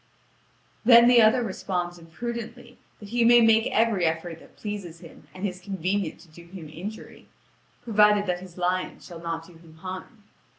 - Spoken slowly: No, average, 170 wpm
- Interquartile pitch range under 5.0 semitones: Yes, average, 4.4 semitones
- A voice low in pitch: No, high, 190 Hz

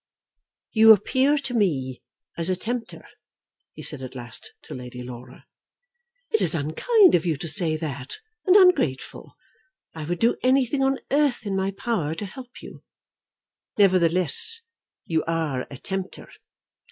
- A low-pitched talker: No, medium, 185 Hz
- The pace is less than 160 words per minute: Yes, average, 145 wpm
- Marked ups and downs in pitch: Yes, wide, 8.7 semitones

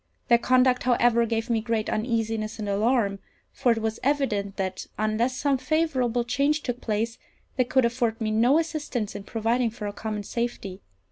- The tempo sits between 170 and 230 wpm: Yes, average, 175 wpm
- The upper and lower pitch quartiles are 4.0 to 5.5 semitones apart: No, average, 2.8 semitones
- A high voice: Yes, high, 235 Hz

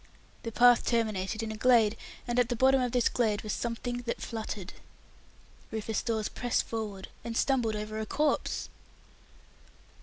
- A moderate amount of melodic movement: No, narrow, 2.1 semitones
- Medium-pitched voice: No, high, 230 Hz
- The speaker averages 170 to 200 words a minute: No, average, 155 wpm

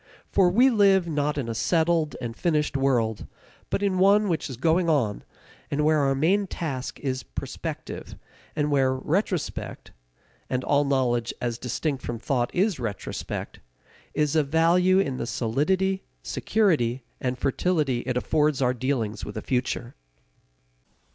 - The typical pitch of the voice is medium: Yes, medium, 145 Hz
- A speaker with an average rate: Yes, average, 150 wpm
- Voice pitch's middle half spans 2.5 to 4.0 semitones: No, average, 5.3 semitones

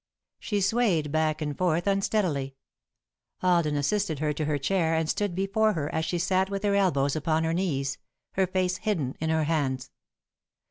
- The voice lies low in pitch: No, medium, 165 Hz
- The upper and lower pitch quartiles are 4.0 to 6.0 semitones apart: Yes, average, 4.3 semitones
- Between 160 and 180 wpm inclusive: Yes, average, 175 wpm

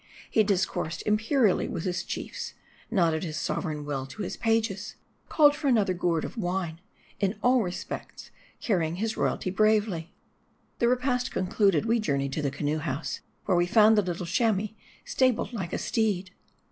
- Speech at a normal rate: Yes, average, 165 wpm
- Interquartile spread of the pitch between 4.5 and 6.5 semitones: Yes, average, 4.9 semitones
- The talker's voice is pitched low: No, high, 195 Hz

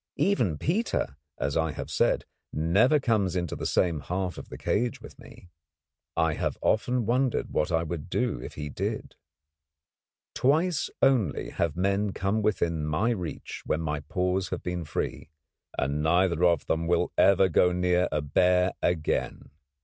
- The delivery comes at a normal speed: Yes, average, 165 wpm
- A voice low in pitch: Yes, very low, 90 Hz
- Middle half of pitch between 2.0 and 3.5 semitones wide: No, average, 4.8 semitones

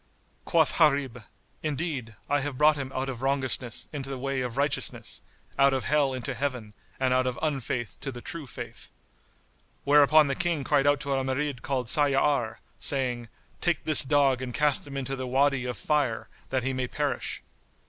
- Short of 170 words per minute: No, average, 180 wpm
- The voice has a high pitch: No, low, 135 Hz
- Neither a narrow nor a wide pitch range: No, narrow, 2.2 semitones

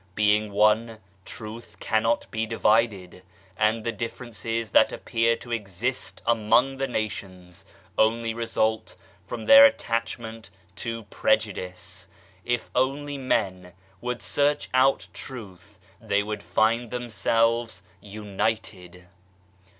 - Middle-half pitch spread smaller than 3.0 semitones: Yes, narrow, 2.4 semitones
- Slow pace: Yes, slow, 105 wpm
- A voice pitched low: Yes, low, 110 Hz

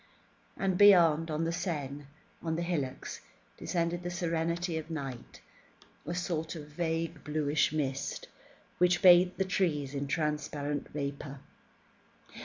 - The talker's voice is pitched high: No, medium, 160 Hz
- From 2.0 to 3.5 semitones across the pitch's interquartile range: Yes, average, 2.9 semitones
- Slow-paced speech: Yes, slow, 125 wpm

